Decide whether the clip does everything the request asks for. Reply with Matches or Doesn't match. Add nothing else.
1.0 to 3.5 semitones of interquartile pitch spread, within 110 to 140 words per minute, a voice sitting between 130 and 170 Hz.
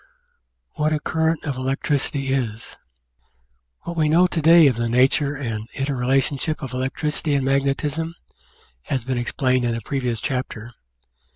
Doesn't match